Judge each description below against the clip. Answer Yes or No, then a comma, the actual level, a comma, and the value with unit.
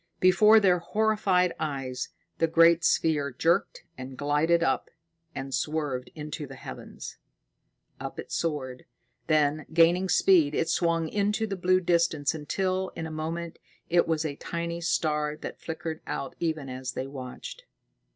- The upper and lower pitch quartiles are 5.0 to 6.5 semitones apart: No, average, 3.1 semitones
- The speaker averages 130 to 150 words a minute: Yes, average, 145 wpm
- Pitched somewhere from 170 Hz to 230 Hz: No, medium, 160 Hz